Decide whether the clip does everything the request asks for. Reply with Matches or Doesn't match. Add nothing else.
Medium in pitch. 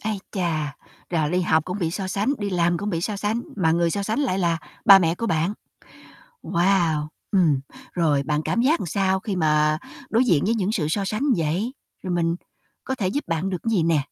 Matches